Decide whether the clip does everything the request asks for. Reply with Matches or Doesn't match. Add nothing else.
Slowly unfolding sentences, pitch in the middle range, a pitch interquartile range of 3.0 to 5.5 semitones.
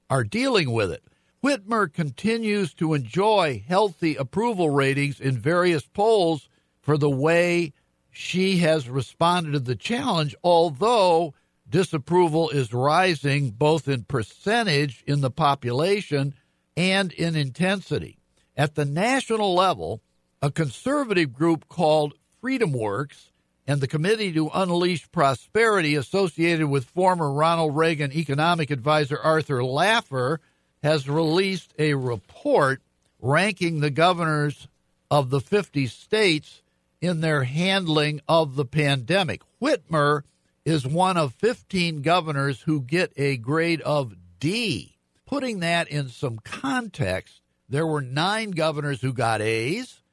Matches